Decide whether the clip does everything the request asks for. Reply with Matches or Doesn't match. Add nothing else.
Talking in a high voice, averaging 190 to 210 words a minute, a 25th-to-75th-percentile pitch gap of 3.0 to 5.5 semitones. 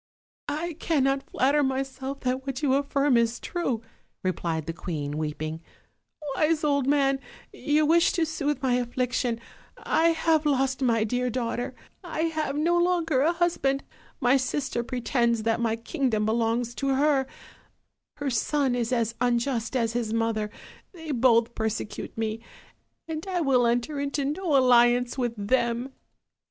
Doesn't match